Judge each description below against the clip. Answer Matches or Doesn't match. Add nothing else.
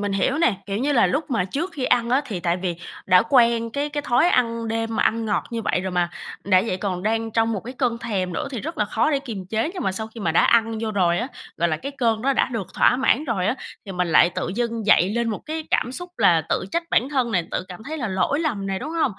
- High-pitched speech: Matches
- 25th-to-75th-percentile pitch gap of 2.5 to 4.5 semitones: Doesn't match